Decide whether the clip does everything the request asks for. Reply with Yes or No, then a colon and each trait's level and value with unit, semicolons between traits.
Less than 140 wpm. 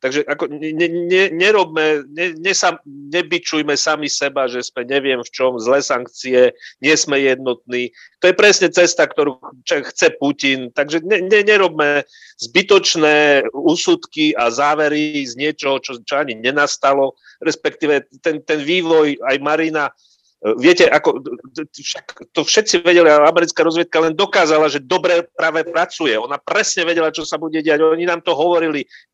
No: average, 145 wpm